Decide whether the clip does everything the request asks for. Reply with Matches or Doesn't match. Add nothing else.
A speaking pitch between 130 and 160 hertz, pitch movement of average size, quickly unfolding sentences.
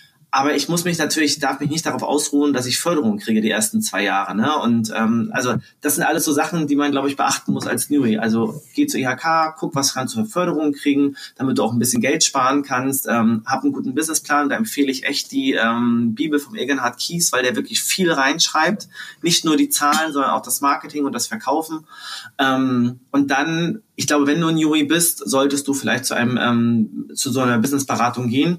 Matches